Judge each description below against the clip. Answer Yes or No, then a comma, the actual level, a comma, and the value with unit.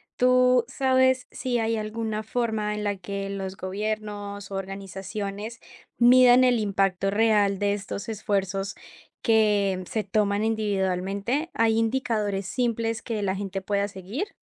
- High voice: Yes, high, 210 Hz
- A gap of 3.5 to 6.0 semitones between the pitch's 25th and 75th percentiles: No, narrow, 2.5 semitones